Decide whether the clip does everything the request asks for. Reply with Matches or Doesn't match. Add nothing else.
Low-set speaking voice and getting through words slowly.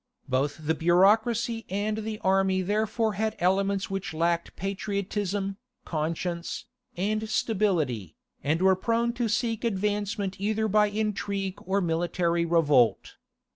Doesn't match